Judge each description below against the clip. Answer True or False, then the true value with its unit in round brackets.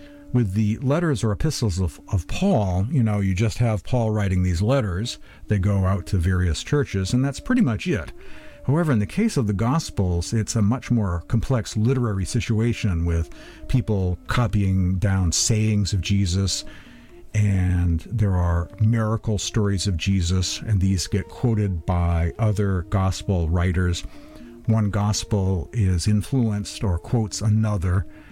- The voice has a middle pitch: False (105 Hz)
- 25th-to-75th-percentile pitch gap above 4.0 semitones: False (3.6 semitones)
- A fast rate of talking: False (150 wpm)